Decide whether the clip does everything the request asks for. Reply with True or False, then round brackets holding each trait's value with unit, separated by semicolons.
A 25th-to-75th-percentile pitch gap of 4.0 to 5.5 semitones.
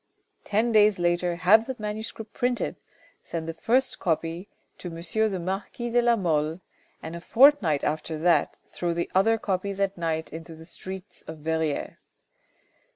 True (4.9 semitones)